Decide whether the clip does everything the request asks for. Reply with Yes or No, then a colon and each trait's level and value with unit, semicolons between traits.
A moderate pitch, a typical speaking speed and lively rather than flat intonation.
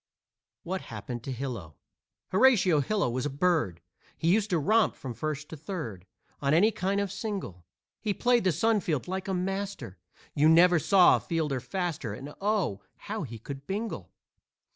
Yes: medium, 170 Hz; average, 170 wpm; wide, 6.7 semitones